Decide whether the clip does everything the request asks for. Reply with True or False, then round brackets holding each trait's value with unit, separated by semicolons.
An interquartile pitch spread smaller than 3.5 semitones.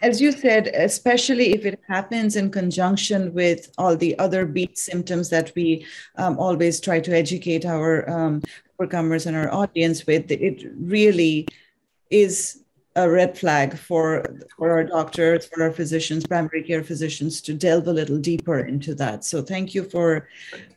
True (2.6 semitones)